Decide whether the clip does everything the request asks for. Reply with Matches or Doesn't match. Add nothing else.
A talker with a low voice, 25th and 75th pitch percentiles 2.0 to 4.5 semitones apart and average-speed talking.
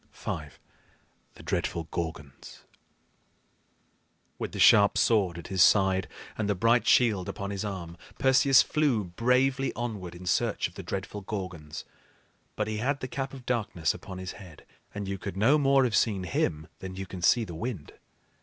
Doesn't match